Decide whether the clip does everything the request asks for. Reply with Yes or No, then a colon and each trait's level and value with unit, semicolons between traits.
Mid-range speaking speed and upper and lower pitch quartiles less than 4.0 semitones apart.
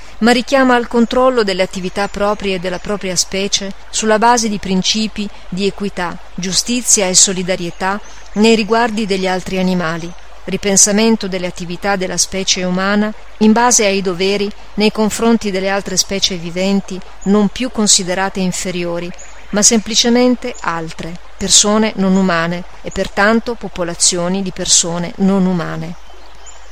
Yes: average, 130 wpm; average, 2.7 semitones